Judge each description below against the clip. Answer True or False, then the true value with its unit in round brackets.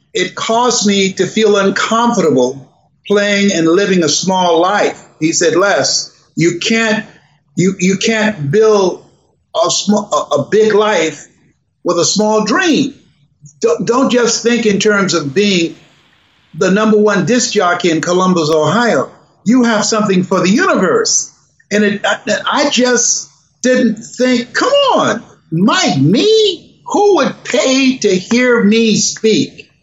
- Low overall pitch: False (205 Hz)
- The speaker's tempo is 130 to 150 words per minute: True (140 wpm)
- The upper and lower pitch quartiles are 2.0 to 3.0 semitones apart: False (4.7 semitones)